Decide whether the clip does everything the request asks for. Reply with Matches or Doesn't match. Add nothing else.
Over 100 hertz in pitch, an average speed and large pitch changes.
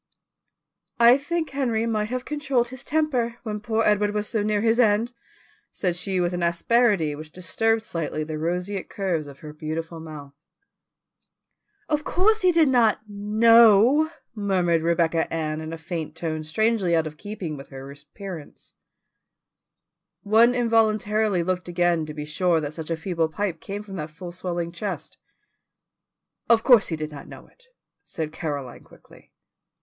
Matches